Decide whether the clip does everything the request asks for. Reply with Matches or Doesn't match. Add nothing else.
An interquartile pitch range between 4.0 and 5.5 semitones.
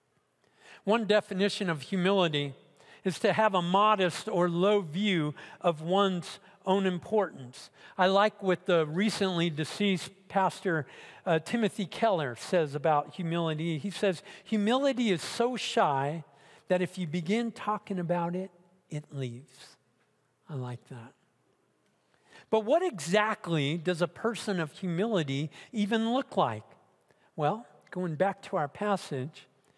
Matches